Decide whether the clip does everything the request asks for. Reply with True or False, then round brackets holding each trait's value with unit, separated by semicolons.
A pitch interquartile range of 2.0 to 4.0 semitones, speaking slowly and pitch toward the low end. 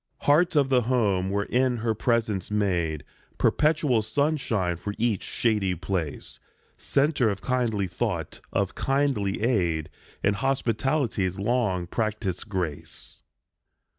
False (5.1 semitones; 110 wpm; 110 Hz)